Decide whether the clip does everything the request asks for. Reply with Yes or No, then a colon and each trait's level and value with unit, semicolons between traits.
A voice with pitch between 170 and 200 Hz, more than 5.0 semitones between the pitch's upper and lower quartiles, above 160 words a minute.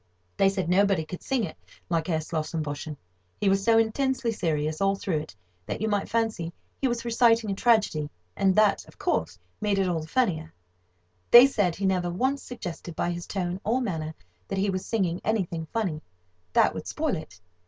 Yes: high, 190 Hz; wide, 5.5 semitones; average, 190 wpm